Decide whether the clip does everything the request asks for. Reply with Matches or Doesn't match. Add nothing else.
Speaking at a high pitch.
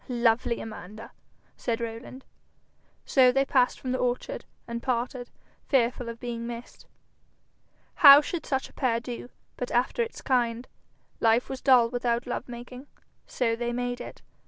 Matches